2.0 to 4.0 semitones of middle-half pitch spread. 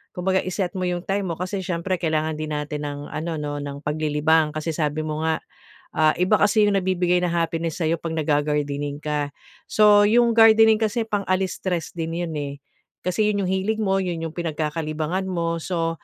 Yes: average, 3.5 semitones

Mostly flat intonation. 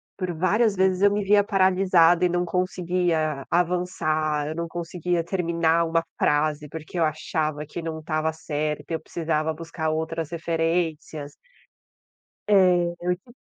Yes: narrow, 2.3 semitones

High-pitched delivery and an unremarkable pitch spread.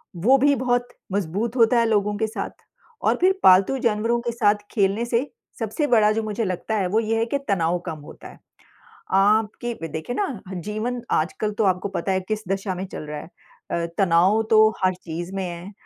Yes: high, 210 Hz; average, 3.6 semitones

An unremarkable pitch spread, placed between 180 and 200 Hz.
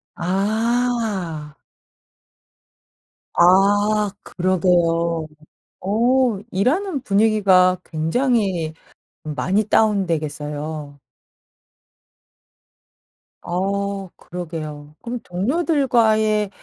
Yes: average, 4.6 semitones; high, 195 Hz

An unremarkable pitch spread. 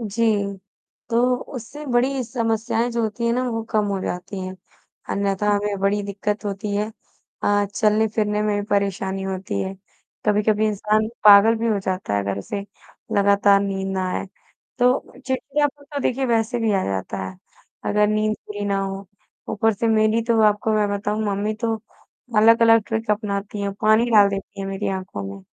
No: narrow, 2.2 semitones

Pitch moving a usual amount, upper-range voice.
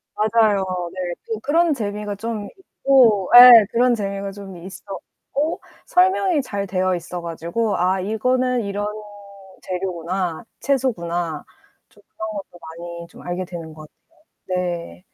Yes: average, 4.7 semitones; high, 200 Hz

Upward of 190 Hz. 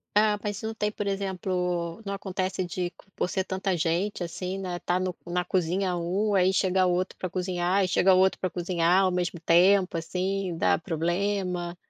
No: medium, 185 Hz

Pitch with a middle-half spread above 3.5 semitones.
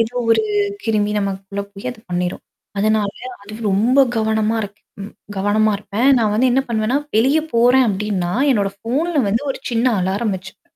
No: average, 2.9 semitones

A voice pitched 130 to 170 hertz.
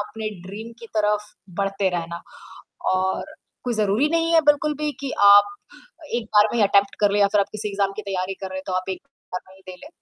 No: high, 205 Hz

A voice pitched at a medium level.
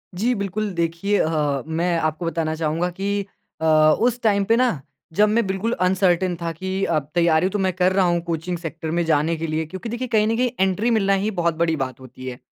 Yes: medium, 175 Hz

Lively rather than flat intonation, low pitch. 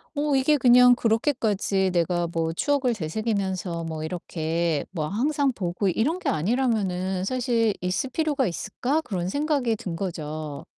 No: wide, 6.7 semitones; high, 200 Hz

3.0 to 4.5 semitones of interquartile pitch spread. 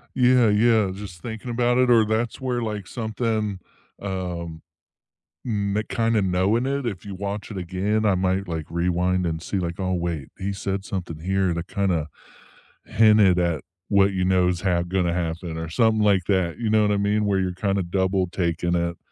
Yes: average, 3.3 semitones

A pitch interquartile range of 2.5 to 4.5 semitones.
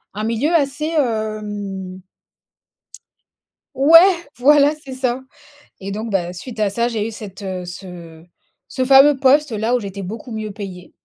No: average, 5.2 semitones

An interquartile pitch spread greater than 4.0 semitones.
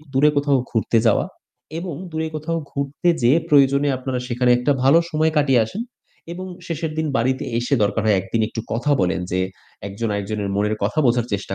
Yes: average, 5.0 semitones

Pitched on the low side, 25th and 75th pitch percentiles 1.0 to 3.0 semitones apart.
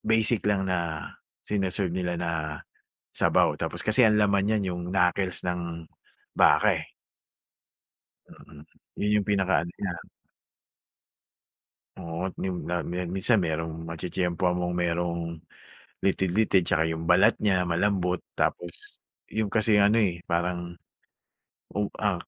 Yes: very low, 90 Hz; narrow, 2.6 semitones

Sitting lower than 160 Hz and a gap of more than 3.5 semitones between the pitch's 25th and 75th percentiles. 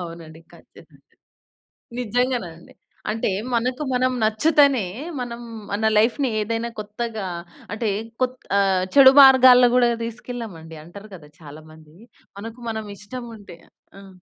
No: high, 225 Hz; average, 4.6 semitones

